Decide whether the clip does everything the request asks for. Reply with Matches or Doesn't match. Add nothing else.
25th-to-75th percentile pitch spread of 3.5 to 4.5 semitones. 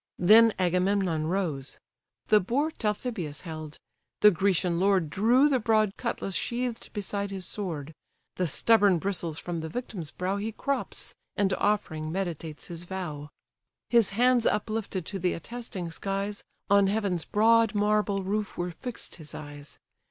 Matches